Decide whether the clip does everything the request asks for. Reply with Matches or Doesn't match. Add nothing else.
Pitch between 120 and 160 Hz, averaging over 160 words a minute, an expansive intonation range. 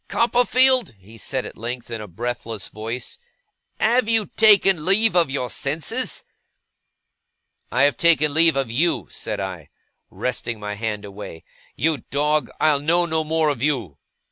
Doesn't match